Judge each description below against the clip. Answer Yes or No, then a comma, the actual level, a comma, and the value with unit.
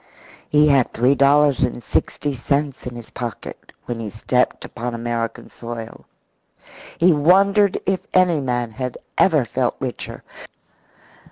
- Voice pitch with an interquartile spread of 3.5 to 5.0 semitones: Yes, average, 3.9 semitones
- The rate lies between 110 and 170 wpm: Yes, slow, 135 wpm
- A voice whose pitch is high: No, low, 130 Hz